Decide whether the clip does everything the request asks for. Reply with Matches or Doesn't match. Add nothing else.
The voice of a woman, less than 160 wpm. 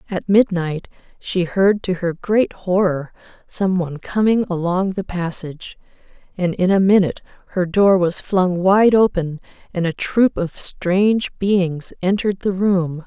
Matches